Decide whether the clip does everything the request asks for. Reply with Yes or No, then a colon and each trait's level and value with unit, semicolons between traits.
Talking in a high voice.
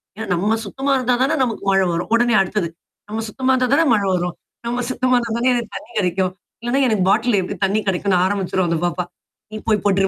Yes: high, 215 Hz